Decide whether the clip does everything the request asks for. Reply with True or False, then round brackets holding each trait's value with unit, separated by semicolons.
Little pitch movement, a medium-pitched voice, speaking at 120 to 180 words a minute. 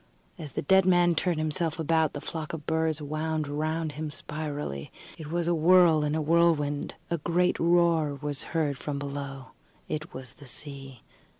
True (2.3 semitones; 155 Hz; 175 wpm)